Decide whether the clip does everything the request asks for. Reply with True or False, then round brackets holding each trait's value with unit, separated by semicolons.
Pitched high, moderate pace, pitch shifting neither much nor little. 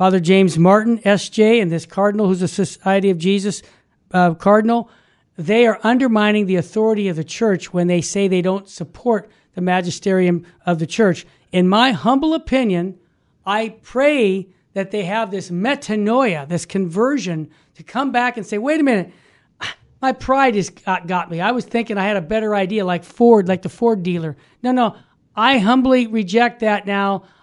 True (200 Hz; 175 wpm; 4.0 semitones)